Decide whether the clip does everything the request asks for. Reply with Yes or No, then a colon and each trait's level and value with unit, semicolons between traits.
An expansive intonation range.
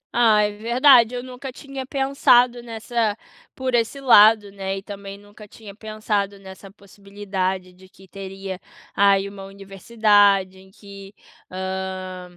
No: average, 3.1 semitones